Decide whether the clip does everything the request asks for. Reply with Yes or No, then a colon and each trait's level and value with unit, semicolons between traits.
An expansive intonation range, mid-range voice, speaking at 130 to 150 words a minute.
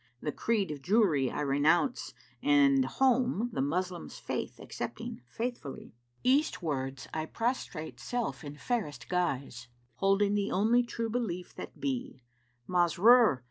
Yes: wide, 8.6 semitones; medium, 180 Hz; slow, 135 wpm